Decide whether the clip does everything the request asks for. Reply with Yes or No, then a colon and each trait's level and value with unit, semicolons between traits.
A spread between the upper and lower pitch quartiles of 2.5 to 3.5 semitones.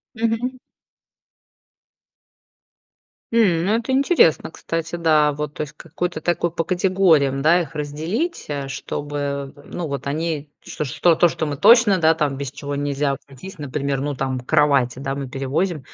No: average, 3.9 semitones